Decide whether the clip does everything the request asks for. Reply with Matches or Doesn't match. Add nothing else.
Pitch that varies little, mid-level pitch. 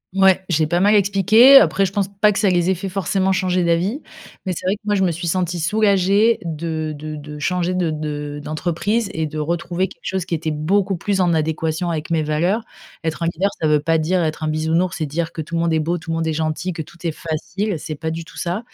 Doesn't match